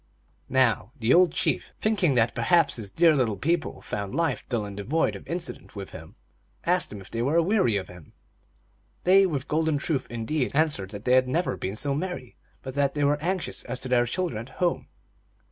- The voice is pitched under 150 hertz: Yes, low, 135 Hz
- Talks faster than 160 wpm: Yes, average, 200 wpm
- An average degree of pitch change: No, wide, 6.6 semitones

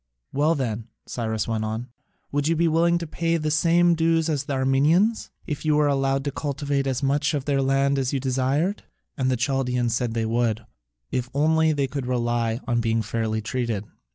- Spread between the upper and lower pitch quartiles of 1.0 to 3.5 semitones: No, average, 4.3 semitones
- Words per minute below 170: No, average, 195 wpm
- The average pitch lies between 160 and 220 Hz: No, low, 135 Hz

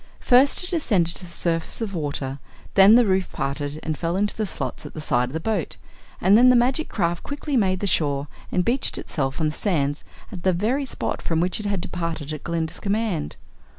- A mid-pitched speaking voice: Yes, medium, 180 Hz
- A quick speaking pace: Yes, fast, 220 wpm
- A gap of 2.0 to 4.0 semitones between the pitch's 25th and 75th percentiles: No, wide, 5.5 semitones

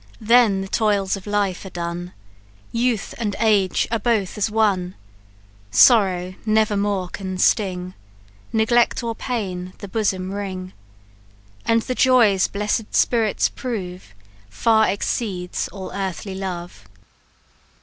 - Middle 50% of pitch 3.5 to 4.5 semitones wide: No, average, 3.0 semitones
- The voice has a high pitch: Yes, high, 200 Hz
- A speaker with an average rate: No, slow, 120 wpm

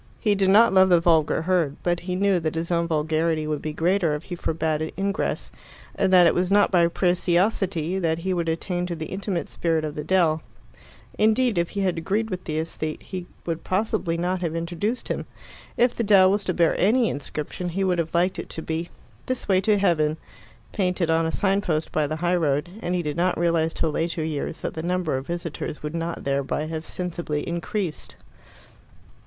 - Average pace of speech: No, fast, 210 wpm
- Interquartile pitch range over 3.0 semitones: No, average, 2.7 semitones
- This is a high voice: No, medium, 170 Hz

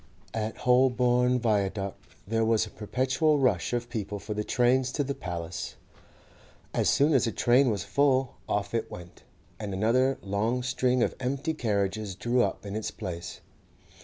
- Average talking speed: Yes, average, 160 wpm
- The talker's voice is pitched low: Yes, low, 115 Hz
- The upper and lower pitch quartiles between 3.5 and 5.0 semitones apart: Yes, average, 3.9 semitones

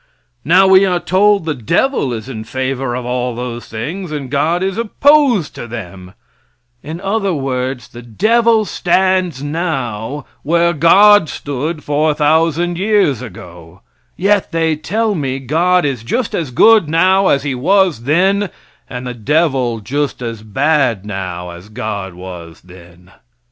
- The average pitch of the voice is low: No, medium, 145 Hz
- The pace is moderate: Yes, average, 145 wpm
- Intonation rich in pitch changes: Yes, wide, 7.3 semitones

